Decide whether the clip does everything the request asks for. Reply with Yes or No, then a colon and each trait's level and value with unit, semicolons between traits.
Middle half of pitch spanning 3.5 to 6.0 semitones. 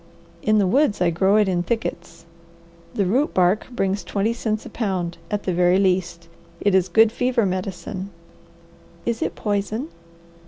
No: average, 3.1 semitones